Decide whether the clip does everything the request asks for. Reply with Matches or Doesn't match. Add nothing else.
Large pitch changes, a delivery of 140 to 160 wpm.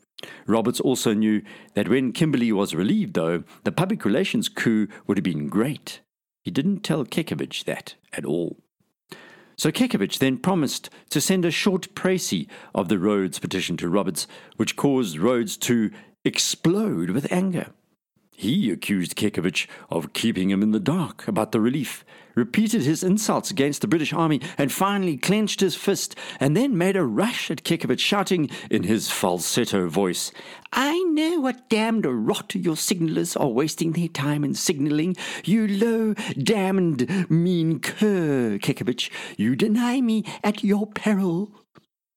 Matches